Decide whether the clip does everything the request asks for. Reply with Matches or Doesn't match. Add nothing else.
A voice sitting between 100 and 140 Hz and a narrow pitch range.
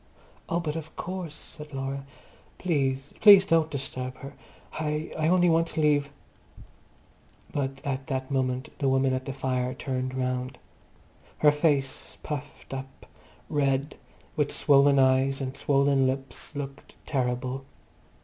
Matches